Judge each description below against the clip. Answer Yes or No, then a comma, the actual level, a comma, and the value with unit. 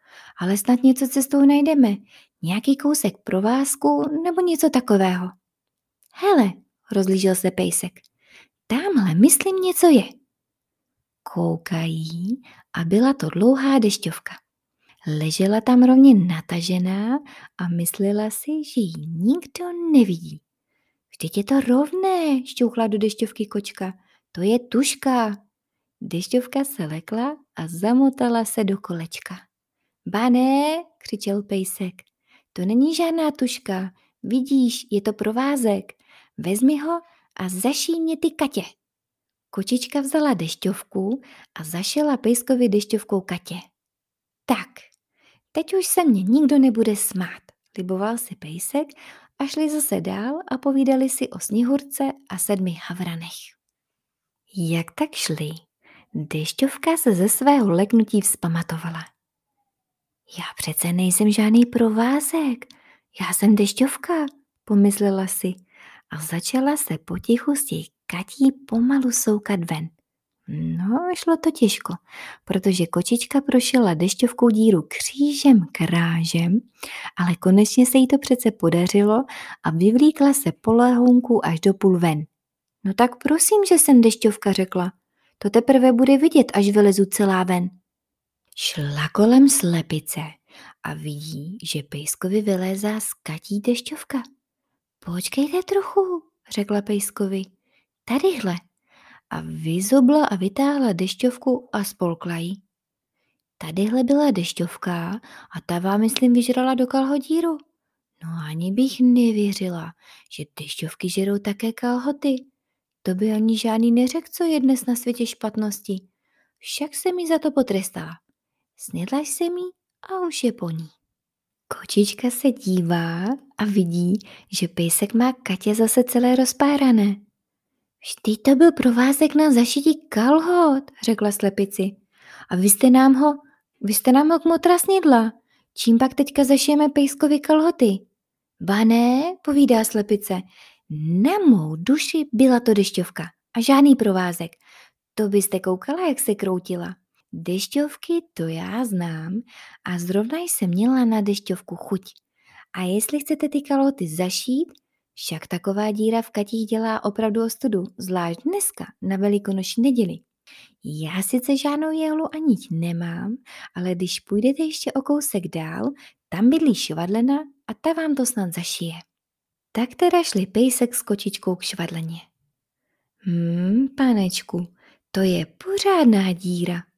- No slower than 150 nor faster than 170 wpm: No, average, 125 wpm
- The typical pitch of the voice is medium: No, high, 220 Hz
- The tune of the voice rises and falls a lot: Yes, wide, 6.6 semitones